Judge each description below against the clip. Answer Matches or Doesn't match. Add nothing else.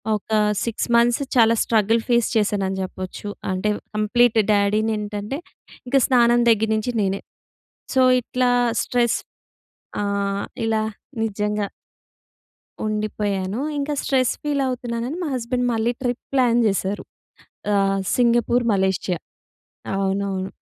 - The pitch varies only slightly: Doesn't match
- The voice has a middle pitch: Doesn't match